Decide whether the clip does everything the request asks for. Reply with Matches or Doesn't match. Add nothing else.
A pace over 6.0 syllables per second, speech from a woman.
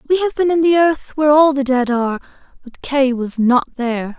Doesn't match